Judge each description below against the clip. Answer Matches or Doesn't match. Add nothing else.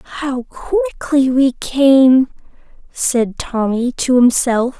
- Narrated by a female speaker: Matches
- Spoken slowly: Matches